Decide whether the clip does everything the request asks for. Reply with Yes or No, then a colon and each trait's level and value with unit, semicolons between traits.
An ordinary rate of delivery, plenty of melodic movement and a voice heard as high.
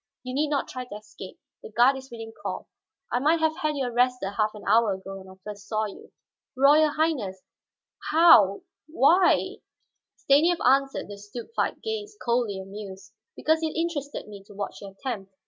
Yes: average, 180 wpm; wide, 6.7 semitones; high, 245 Hz